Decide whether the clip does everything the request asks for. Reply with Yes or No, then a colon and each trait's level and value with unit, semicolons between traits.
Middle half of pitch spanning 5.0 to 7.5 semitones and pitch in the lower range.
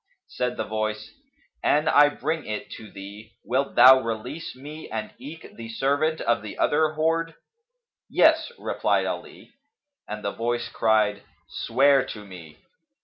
Yes: average, 5.3 semitones; low, 125 Hz